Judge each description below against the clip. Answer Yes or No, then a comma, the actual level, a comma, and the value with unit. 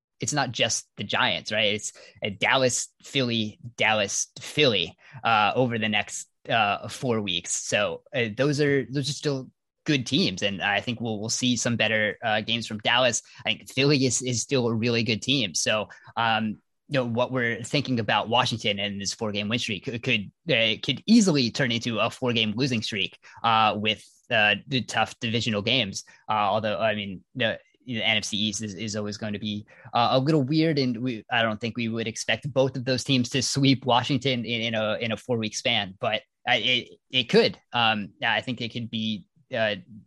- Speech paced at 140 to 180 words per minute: No, fast, 205 wpm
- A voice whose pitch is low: Yes, low, 115 Hz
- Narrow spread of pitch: No, average, 3.0 semitones